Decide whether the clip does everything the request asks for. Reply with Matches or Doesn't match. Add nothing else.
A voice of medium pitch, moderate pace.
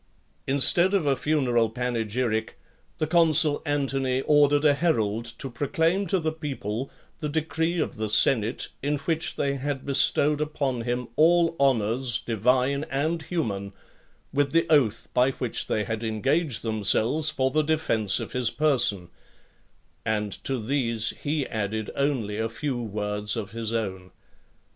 Doesn't match